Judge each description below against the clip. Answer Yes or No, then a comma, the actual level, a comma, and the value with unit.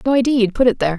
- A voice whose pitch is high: Yes, high, 230 Hz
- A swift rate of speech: Yes, fast, 365 wpm